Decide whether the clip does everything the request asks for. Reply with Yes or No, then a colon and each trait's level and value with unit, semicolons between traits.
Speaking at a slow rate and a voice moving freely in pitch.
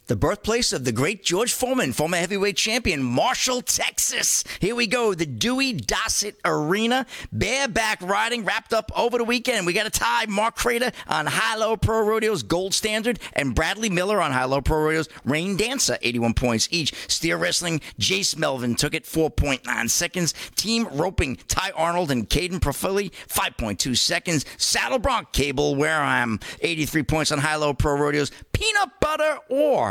No: average, 170 wpm; wide, 7.1 semitones